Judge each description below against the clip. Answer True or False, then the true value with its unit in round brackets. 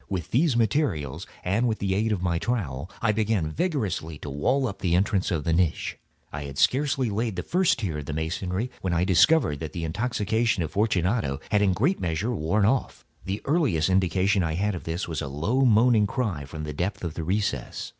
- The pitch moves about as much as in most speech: False (5.7 semitones)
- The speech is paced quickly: True (215 wpm)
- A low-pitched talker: True (95 Hz)